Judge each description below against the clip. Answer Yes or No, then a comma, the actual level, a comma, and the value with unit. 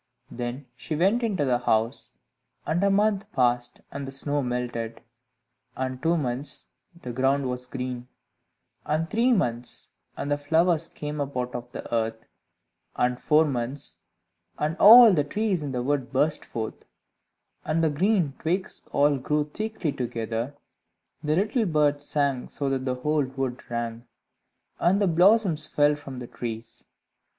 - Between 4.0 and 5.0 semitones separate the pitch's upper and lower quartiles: Yes, average, 4.7 semitones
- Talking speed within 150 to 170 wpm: Yes, average, 155 wpm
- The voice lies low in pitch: No, medium, 145 Hz